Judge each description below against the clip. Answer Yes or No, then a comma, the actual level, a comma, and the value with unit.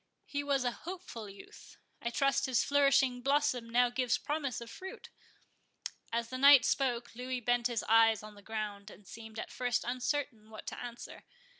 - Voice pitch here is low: No, high, 245 Hz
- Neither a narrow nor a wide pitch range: Yes, average, 3.3 semitones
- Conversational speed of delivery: Yes, average, 175 wpm